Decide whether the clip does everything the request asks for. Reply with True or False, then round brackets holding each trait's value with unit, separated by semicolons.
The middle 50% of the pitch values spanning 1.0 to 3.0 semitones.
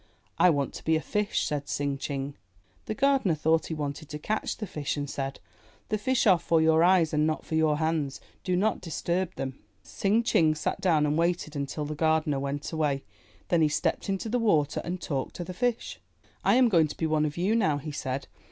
False (3.8 semitones)